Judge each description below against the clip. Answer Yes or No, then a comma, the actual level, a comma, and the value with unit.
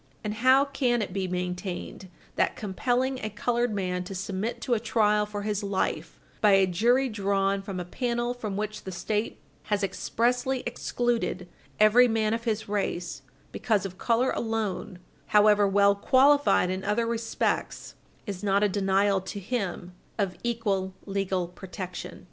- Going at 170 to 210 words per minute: No, average, 155 wpm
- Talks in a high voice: Yes, high, 210 Hz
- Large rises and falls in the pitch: No, average, 3.3 semitones